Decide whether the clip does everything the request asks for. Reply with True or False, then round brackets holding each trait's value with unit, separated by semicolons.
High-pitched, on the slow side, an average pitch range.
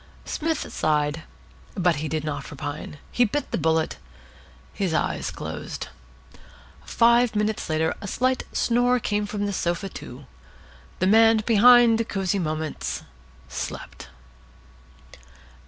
False (200 Hz; 120 wpm; 6.4 semitones)